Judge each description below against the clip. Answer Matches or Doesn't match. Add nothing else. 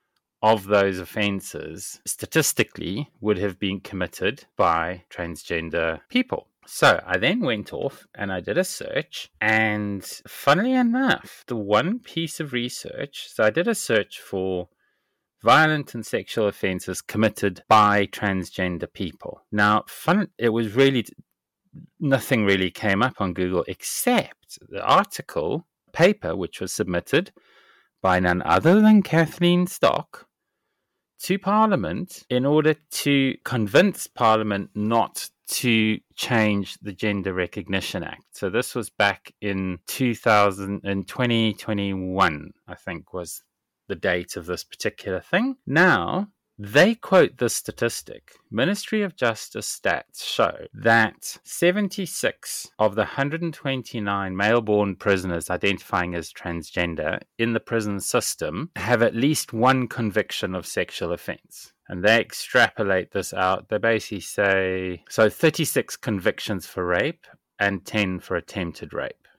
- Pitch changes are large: Matches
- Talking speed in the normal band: Doesn't match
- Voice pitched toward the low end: Matches